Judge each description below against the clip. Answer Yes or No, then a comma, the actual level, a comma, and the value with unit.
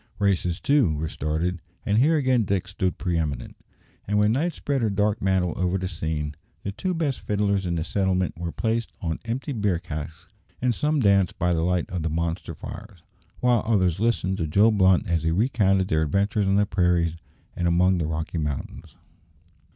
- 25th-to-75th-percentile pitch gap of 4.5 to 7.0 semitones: No, average, 3.9 semitones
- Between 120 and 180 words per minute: No, average, 190 wpm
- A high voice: No, very low, 95 Hz